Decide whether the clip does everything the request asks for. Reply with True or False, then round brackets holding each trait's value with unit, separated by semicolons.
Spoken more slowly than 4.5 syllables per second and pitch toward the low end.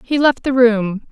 False (4.1 syllables/s; 240 Hz)